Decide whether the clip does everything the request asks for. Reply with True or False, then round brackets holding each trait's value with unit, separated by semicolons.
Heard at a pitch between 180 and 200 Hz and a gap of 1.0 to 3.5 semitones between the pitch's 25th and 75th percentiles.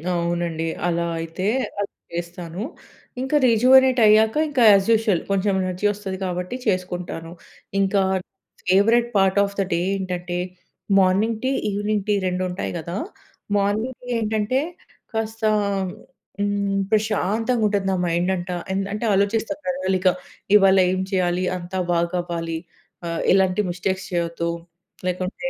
True (190 Hz; 3.1 semitones)